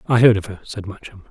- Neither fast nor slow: No, fast, 275 wpm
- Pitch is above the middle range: No, low, 105 Hz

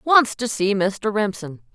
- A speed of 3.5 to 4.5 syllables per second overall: Yes, 3.8 syllables/s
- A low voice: No, high, 210 Hz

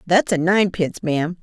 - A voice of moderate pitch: Yes, medium, 175 Hz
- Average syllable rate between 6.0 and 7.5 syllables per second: Yes, 6.2 syllables/s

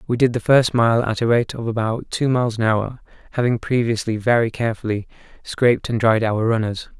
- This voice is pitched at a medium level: No, low, 115 Hz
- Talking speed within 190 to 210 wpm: Yes, average, 195 wpm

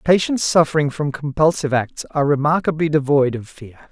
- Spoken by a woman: No, male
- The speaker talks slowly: No, average, 155 wpm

